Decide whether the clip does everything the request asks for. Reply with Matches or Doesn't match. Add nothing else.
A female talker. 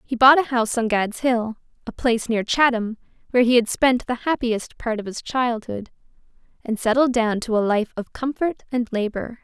Matches